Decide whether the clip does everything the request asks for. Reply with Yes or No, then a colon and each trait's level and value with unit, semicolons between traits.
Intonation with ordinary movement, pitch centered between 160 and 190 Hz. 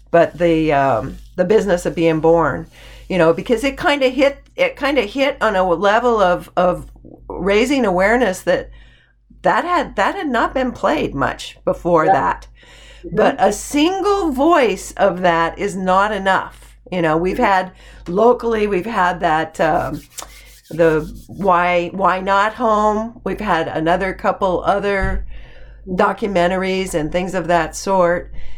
Yes: average, 4.1 semitones; medium, 185 Hz